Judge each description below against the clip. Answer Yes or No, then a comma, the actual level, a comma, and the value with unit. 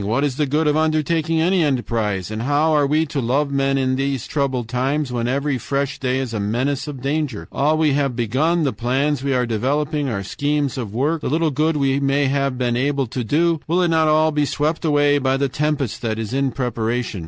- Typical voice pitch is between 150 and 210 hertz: No, medium, 140 Hz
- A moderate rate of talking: No, fast, 225 wpm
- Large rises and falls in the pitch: No, average, 3.1 semitones